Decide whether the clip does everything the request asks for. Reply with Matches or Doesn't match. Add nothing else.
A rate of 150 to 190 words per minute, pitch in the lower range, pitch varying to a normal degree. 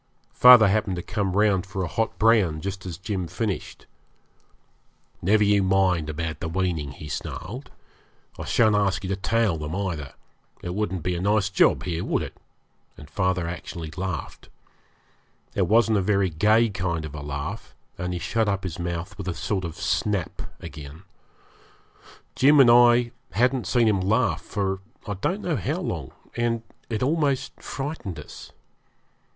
Matches